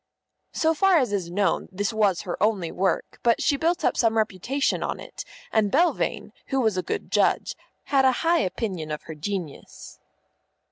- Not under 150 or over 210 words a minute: Yes, average, 185 wpm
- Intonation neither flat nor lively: No, wide, 6.5 semitones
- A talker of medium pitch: No, high, 215 Hz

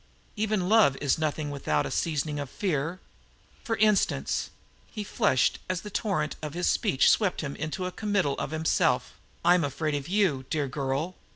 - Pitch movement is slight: No, wide, 5.4 semitones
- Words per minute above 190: No, average, 175 wpm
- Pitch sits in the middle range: Yes, medium, 160 Hz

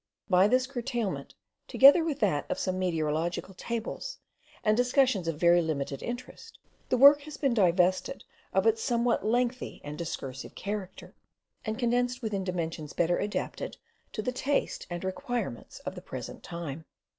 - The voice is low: No, high, 210 Hz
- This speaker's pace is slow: No, average, 150 wpm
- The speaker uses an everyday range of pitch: No, wide, 6.2 semitones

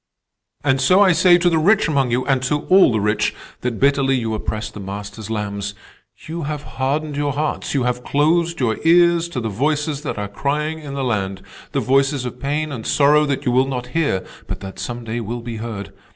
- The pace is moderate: No, fast, 210 wpm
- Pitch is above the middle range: No, low, 135 Hz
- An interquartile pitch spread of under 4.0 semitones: No, average, 5.1 semitones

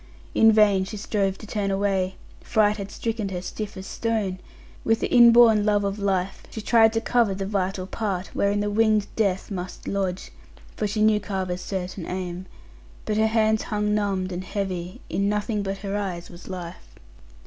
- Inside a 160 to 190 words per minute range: Yes, average, 180 wpm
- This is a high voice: Yes, high, 200 Hz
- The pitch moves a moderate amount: No, narrow, 2.2 semitones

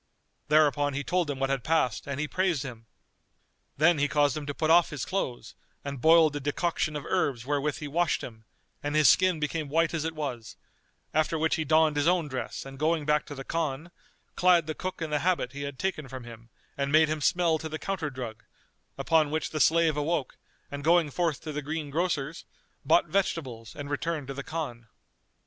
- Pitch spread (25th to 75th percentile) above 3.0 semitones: No, average, 2.7 semitones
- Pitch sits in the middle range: Yes, medium, 150 Hz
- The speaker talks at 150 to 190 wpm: No, fast, 205 wpm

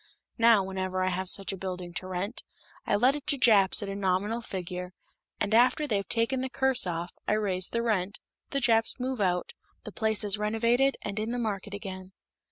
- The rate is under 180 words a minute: No, average, 200 wpm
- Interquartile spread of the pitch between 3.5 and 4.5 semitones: Yes, average, 3.8 semitones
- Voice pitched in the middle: No, high, 205 Hz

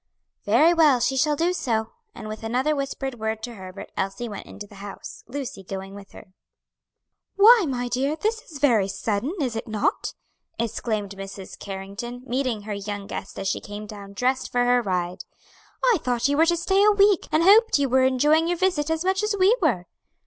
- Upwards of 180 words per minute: Yes, average, 200 wpm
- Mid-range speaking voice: No, high, 245 Hz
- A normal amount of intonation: No, wide, 7.3 semitones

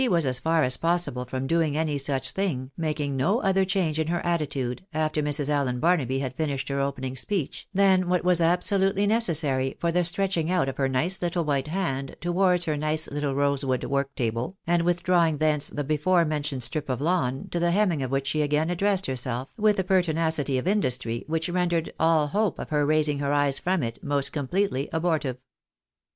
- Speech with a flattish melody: No, average, 4.3 semitones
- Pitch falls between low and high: Yes, medium, 155 Hz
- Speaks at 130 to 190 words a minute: No, average, 200 wpm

